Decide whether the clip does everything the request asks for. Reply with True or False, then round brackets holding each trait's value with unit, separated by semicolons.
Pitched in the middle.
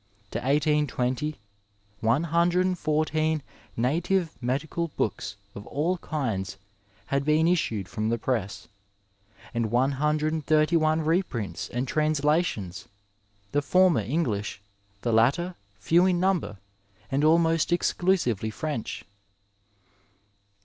True (150 Hz)